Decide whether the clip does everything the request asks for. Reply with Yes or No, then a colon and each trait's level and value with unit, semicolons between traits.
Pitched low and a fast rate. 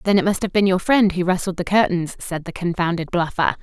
No: medium, 180 Hz; fast, 250 wpm